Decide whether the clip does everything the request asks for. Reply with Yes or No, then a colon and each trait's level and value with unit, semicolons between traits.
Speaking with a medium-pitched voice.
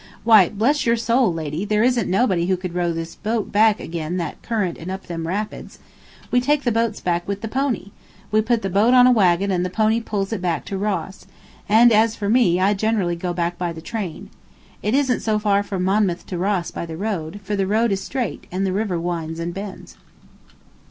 No: high, 200 Hz